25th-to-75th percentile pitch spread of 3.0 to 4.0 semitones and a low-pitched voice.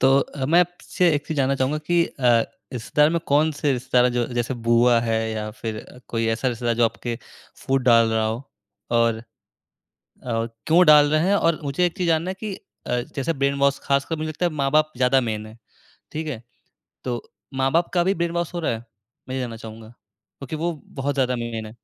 No: average, 4.8 semitones; low, 130 Hz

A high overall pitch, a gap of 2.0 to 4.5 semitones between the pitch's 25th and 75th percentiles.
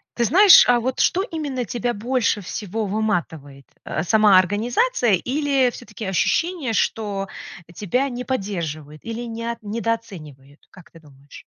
No: high, 220 Hz; average, 5.3 semitones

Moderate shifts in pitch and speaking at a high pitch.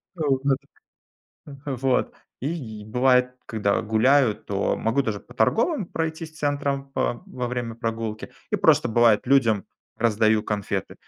No: average, 4.0 semitones; low, 125 Hz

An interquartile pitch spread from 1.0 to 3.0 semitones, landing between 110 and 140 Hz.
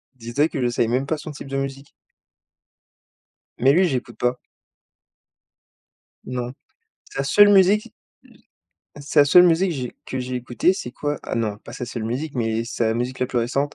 No: average, 3.4 semitones; low, 130 Hz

